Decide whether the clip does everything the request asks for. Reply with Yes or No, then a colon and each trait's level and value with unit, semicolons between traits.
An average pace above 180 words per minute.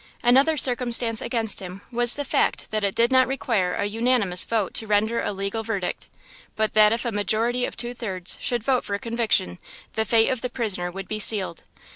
Yes: average, 200 wpm